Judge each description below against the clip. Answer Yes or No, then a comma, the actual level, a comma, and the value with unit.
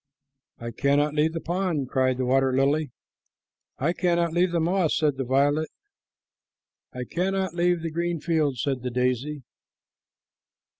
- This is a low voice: No, medium, 150 Hz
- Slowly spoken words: No, average, 145 wpm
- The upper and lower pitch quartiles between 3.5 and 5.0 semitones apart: Yes, average, 4.4 semitones